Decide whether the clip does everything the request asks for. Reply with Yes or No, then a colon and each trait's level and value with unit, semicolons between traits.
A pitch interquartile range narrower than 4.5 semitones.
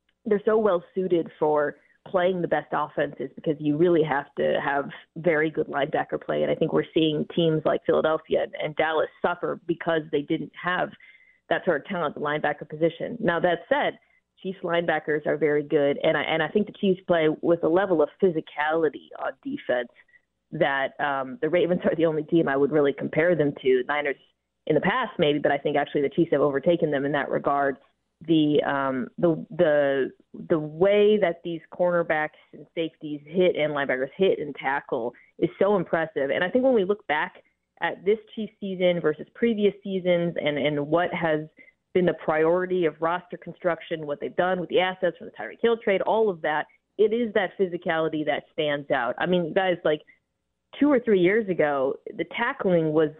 Yes: average, 3.9 semitones